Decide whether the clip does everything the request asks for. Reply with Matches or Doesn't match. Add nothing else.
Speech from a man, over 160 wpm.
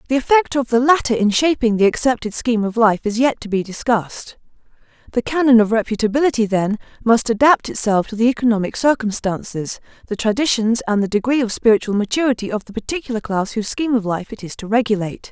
Doesn't match